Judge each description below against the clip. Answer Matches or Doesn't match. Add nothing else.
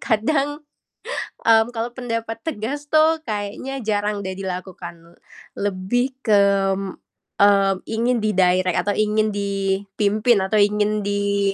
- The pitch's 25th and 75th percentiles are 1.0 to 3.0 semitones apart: Matches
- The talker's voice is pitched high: Matches